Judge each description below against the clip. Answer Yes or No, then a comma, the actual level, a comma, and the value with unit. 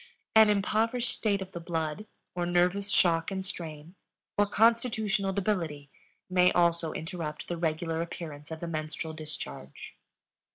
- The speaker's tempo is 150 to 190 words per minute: No, slow, 135 wpm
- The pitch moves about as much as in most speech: Yes, average, 3.9 semitones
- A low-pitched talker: No, medium, 175 Hz